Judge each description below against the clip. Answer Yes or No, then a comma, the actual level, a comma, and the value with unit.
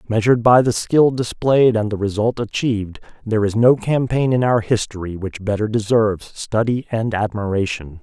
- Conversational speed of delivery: Yes, average, 165 wpm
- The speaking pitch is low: Yes, low, 110 Hz